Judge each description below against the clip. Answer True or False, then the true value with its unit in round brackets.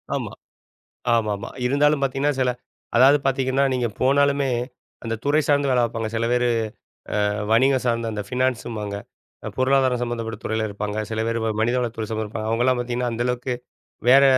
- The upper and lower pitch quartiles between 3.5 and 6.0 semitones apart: False (2.9 semitones)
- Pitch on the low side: True (125 Hz)